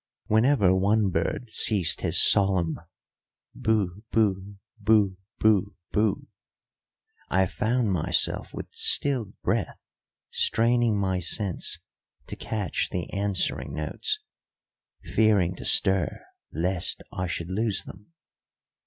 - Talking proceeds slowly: Yes, slow, 105 wpm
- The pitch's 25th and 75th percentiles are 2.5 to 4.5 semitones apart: Yes, average, 2.9 semitones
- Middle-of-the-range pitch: No, low, 100 Hz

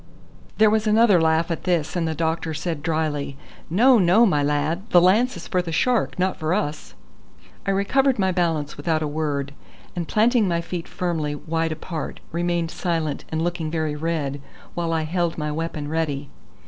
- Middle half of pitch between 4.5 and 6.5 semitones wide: No, average, 2.8 semitones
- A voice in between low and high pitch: Yes, medium, 165 Hz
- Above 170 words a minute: Yes, average, 180 wpm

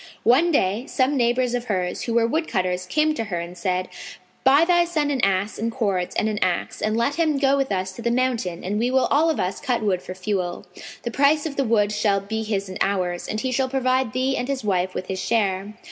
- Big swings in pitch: Yes, wide, 5.8 semitones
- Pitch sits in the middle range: No, high, 225 Hz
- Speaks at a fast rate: Yes, fast, 240 wpm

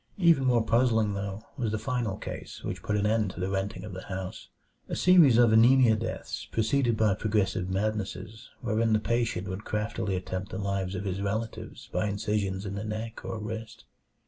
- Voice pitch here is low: Yes, low, 105 Hz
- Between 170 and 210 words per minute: Yes, average, 190 wpm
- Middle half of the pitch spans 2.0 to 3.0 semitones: Yes, narrow, 2.6 semitones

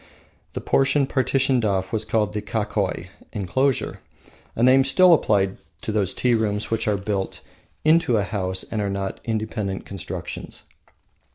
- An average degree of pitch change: Yes, average, 4.2 semitones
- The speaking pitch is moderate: No, low, 110 Hz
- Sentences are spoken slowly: No, average, 150 wpm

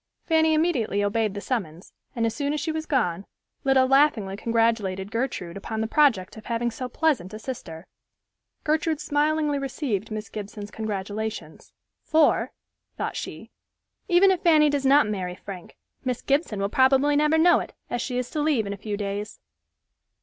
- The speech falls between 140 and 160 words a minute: No, average, 170 wpm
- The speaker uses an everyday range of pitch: No, wide, 6.3 semitones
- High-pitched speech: Yes, high, 235 Hz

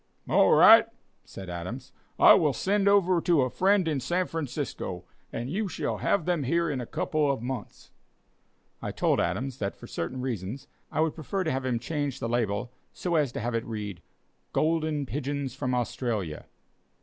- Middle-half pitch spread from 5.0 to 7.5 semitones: Yes, average, 5.3 semitones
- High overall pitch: No, low, 135 Hz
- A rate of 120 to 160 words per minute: No, average, 180 wpm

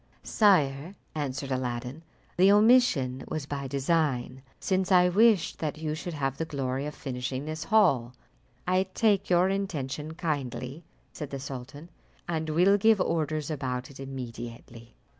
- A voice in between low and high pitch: Yes, medium, 150 Hz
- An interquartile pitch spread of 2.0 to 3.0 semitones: No, average, 5.2 semitones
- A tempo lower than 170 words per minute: Yes, average, 140 wpm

